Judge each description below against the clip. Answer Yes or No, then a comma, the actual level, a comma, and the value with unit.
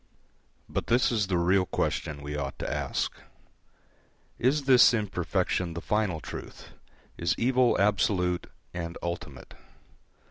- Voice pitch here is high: No, very low, 90 Hz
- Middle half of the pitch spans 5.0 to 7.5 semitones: No, average, 4.3 semitones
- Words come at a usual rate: No, slow, 120 wpm